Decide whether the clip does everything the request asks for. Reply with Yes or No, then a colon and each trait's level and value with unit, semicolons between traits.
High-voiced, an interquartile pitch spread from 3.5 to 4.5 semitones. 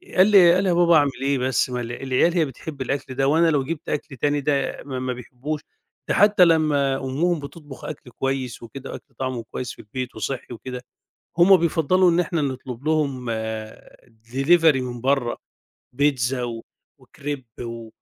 No: low, 135 Hz; average, 3.9 semitones